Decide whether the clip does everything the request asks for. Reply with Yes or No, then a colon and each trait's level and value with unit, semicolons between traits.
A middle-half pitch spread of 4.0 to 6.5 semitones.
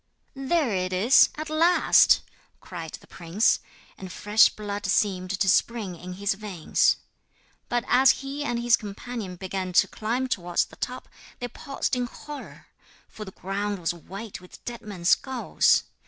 Yes: average, 4.8 semitones